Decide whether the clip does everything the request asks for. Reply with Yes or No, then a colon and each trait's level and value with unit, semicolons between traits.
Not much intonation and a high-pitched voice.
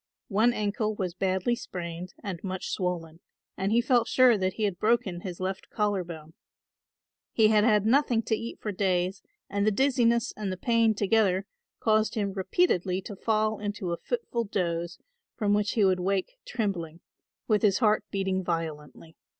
No: average, 3.2 semitones; high, 200 Hz